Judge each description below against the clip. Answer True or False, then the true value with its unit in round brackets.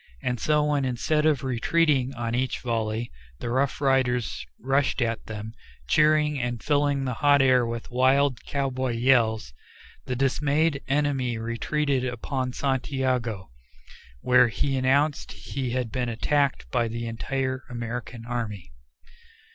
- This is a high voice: False (130 Hz)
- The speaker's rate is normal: False (130 wpm)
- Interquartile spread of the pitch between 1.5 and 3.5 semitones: True (2.9 semitones)